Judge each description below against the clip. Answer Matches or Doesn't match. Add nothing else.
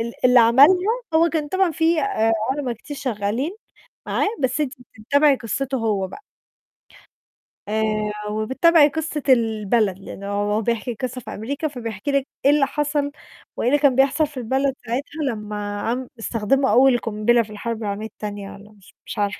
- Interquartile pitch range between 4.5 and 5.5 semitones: Matches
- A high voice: Matches